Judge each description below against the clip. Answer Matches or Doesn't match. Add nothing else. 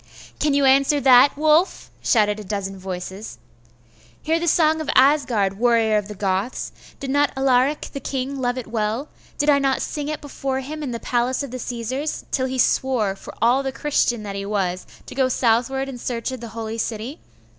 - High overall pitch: Matches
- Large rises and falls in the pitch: Doesn't match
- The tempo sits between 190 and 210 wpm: Matches